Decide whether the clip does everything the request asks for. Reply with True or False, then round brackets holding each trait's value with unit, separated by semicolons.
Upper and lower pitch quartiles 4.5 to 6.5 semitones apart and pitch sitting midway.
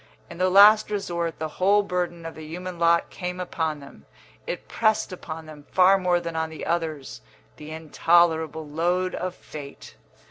False (2.4 semitones; 170 Hz)